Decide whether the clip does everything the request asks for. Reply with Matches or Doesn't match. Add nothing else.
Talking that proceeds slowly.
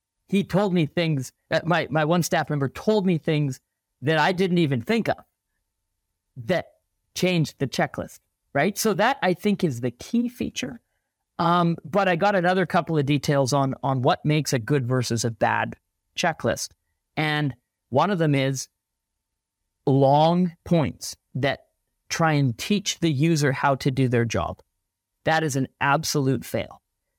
Doesn't match